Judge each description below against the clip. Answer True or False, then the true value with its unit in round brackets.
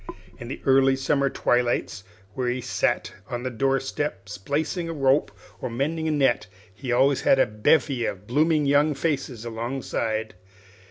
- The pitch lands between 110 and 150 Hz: True (135 Hz)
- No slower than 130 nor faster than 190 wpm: True (160 wpm)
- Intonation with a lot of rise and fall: False (3.2 semitones)